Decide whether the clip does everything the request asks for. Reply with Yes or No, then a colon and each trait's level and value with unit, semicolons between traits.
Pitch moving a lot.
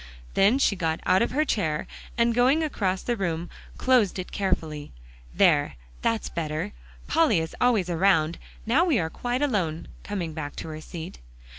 Yes: wide, 6.8 semitones